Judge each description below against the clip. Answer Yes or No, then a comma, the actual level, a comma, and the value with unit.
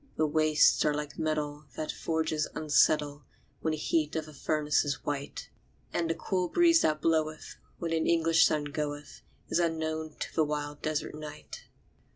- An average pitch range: No, narrow, 1.3 semitones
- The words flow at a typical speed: Yes, average, 170 wpm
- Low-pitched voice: No, medium, 155 Hz